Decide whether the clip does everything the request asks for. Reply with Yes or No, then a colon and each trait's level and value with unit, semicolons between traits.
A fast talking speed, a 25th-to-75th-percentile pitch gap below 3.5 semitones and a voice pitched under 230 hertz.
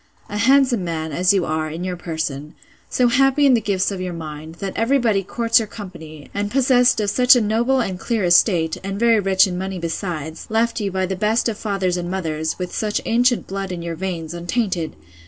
No: fast, 215 wpm; average, 4.9 semitones; high, 190 Hz